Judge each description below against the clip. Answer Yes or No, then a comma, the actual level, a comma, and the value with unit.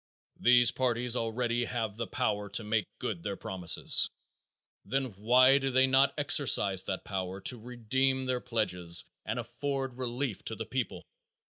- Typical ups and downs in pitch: Yes, average, 3.7 semitones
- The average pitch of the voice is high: No, low, 120 Hz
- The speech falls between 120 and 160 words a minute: Yes, average, 150 wpm